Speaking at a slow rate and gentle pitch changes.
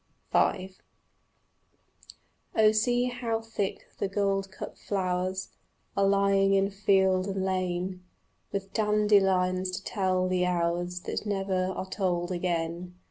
Yes: slow, 115 wpm; narrow, 1.5 semitones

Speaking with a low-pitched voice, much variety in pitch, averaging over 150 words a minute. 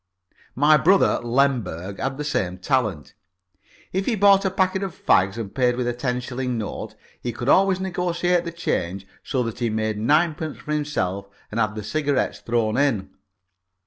Yes: low, 130 Hz; wide, 7.0 semitones; average, 175 wpm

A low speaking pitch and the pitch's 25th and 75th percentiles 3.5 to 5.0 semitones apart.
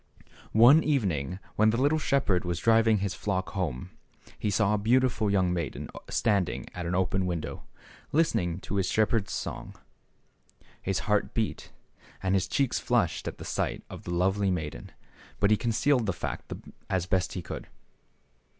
Yes: low, 100 Hz; average, 3.8 semitones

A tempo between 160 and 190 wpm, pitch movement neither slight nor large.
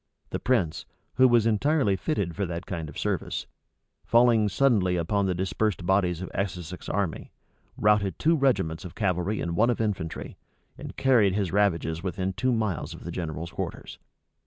Yes: average, 165 wpm; average, 4.1 semitones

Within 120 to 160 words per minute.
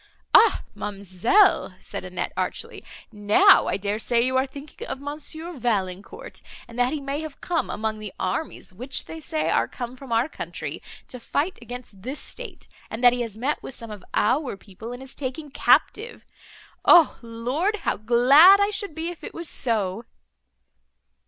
No: average, 175 wpm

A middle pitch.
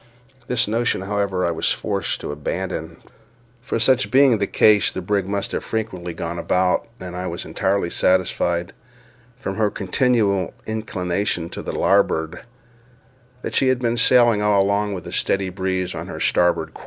No: very low, 95 Hz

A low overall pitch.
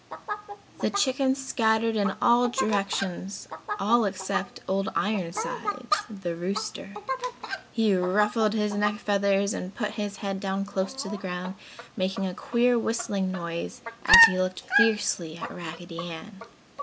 No: high, 200 Hz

